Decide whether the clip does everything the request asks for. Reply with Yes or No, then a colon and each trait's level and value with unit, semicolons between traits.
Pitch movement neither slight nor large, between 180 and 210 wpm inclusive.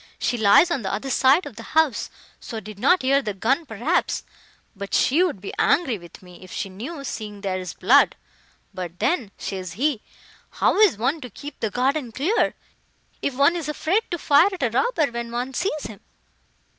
No: wide, 6.9 semitones; average, 195 wpm